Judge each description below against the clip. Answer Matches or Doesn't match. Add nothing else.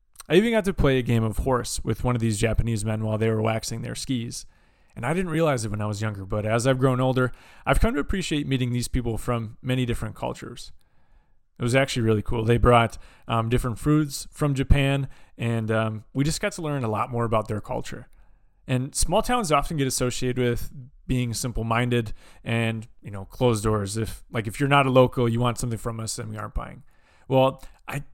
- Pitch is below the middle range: Matches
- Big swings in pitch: Doesn't match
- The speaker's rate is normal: Doesn't match